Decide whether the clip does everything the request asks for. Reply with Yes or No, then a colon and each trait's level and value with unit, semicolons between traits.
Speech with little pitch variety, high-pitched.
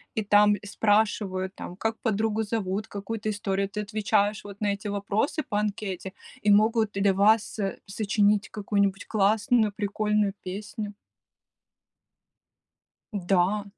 Yes: narrow, 1.4 semitones; high, 205 Hz